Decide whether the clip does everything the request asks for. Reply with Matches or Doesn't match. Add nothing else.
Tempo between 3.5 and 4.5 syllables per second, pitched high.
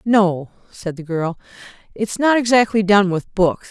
Matches